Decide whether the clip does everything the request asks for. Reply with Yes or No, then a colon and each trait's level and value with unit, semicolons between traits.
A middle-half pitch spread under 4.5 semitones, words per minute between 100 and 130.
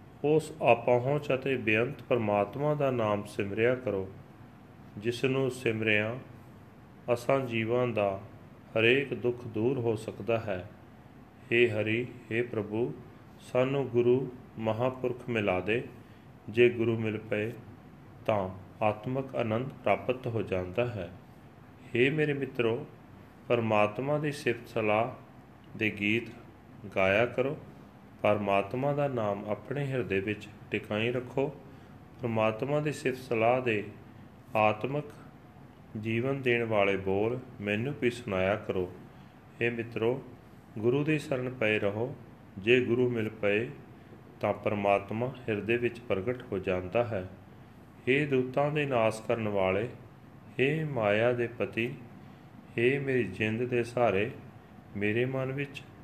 Yes: average, 2.9 semitones; average, 120 wpm